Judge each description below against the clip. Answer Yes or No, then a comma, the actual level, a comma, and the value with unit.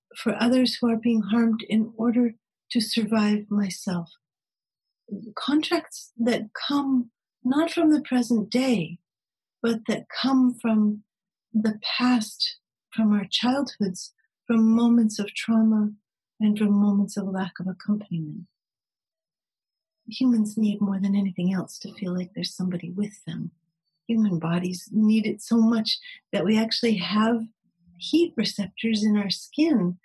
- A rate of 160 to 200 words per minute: No, slow, 135 wpm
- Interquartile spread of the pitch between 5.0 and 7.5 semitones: No, average, 3.0 semitones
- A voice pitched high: Yes, high, 215 Hz